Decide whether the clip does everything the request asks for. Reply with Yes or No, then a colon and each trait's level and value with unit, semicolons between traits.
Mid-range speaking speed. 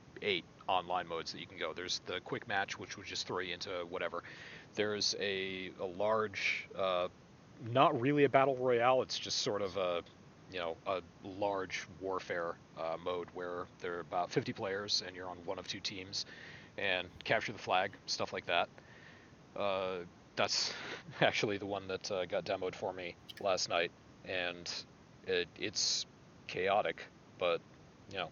Yes: average, 165 wpm